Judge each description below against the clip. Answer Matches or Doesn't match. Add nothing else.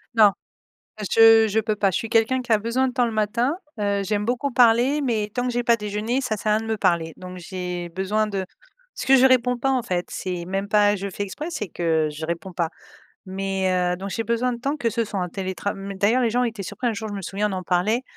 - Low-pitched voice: Doesn't match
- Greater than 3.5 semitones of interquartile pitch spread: Matches